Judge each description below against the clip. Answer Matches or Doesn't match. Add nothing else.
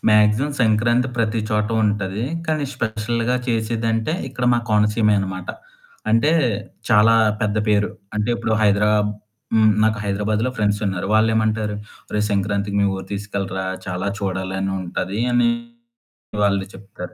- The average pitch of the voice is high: Doesn't match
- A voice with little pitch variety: Matches